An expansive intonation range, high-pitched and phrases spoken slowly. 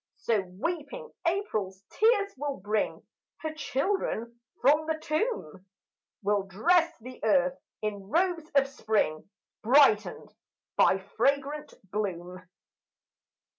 Yes: wide, 7.8 semitones; very high, 270 Hz; slow, 100 wpm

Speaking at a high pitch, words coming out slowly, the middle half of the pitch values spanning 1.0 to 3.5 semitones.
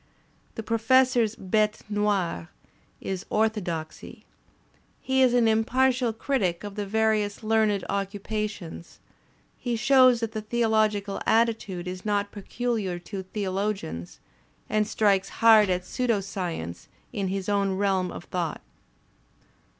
Yes: high, 210 Hz; slow, 120 wpm; average, 2.7 semitones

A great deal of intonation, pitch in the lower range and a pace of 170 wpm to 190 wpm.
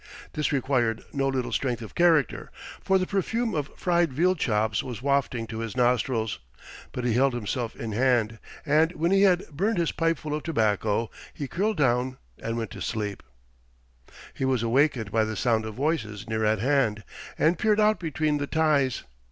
Yes: wide, 5.9 semitones; low, 130 Hz; average, 180 wpm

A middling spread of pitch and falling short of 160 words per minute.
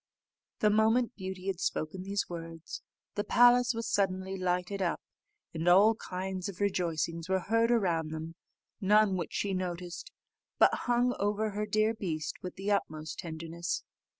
Yes: average, 3.6 semitones; average, 150 wpm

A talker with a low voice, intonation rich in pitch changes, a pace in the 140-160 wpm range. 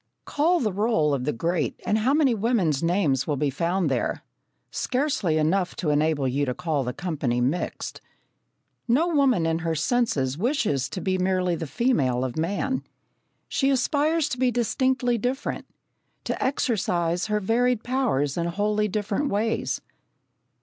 No: high, 190 Hz; wide, 8.1 semitones; average, 155 wpm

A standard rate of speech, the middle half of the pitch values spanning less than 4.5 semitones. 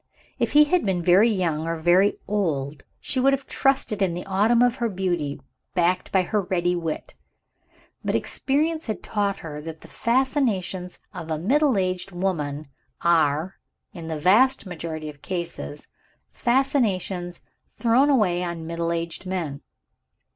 No: average, 155 wpm; average, 5.3 semitones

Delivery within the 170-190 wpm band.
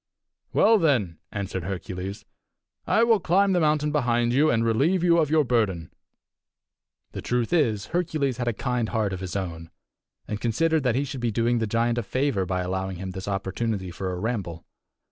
Yes: average, 185 wpm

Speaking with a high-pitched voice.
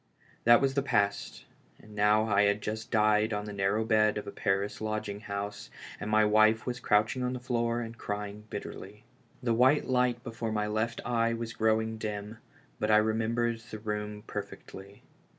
No: low, 110 Hz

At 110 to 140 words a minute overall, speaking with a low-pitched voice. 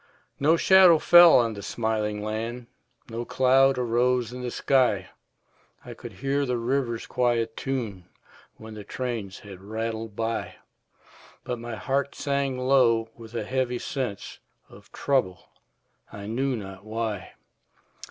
Yes: slow, 135 wpm; low, 120 Hz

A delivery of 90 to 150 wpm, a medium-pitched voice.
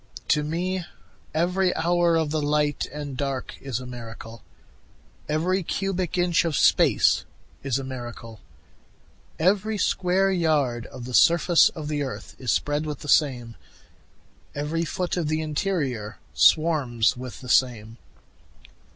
Yes: slow, 135 wpm; medium, 150 Hz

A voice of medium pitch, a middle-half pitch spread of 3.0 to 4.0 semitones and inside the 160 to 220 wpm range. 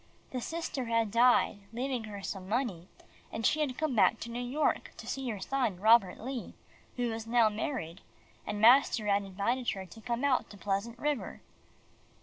No: high, 230 Hz; average, 3.6 semitones; average, 180 wpm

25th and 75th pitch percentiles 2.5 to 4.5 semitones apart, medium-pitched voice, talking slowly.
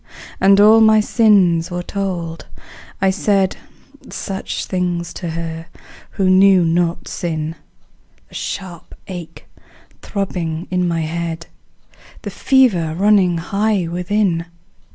Yes: average, 2.8 semitones; medium, 180 Hz; slow, 110 wpm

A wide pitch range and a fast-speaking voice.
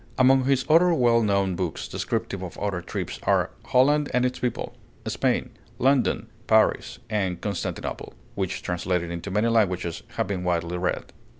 No: wide, 6.0 semitones; average, 155 wpm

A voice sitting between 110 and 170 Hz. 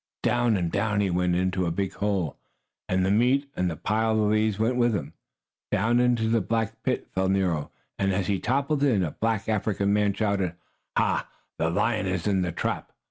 No: low, 100 Hz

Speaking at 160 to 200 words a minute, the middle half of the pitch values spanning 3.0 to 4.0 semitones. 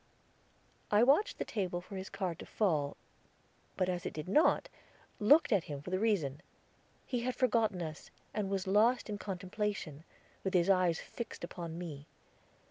Yes: average, 165 wpm; average, 3.6 semitones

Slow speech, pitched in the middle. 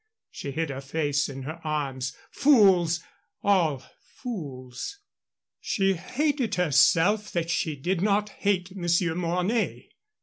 Yes: slow, 115 wpm; medium, 170 Hz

